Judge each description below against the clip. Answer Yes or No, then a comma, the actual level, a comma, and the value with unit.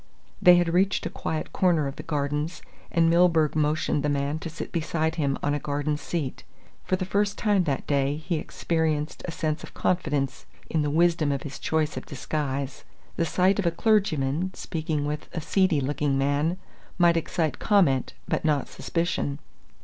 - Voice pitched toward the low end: No, medium, 155 Hz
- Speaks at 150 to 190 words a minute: Yes, average, 180 wpm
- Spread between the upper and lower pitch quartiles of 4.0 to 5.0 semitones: No, average, 3.0 semitones